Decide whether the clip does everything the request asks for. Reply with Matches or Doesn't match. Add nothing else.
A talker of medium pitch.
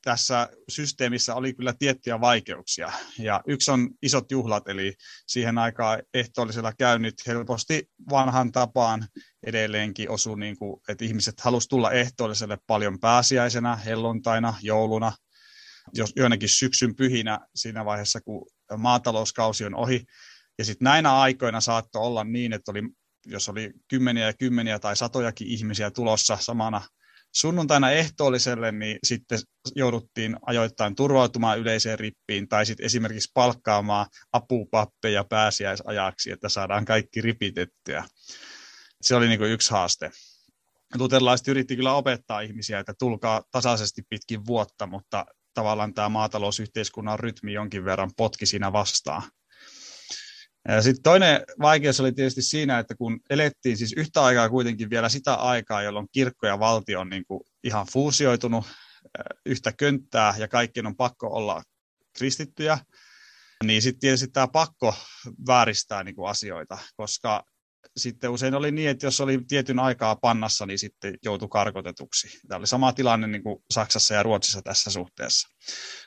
Doesn't match